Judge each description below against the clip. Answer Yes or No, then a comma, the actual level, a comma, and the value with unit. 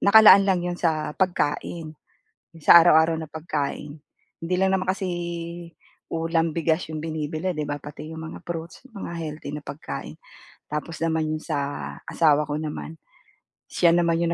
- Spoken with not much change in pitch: Yes, narrow, 2.1 semitones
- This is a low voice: No, medium, 160 Hz